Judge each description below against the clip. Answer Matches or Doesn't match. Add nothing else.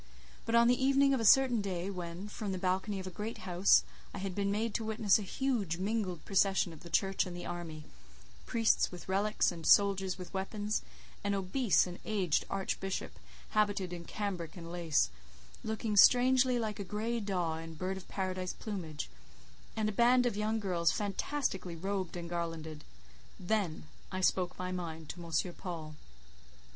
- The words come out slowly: Doesn't match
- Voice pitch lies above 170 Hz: Matches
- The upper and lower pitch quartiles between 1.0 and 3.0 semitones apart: Doesn't match